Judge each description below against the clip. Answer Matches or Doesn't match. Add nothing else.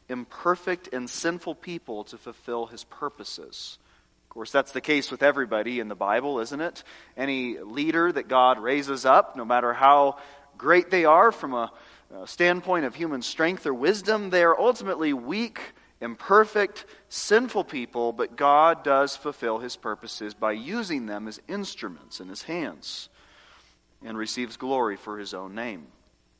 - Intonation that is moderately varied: Doesn't match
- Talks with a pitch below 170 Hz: Matches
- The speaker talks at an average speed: Matches